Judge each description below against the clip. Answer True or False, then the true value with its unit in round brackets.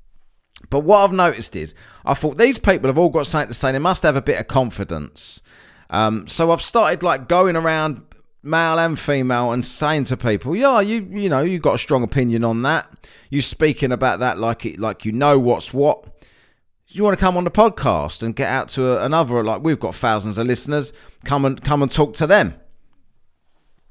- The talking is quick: True (210 wpm)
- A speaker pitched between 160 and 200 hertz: False (140 Hz)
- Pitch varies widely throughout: True (5.9 semitones)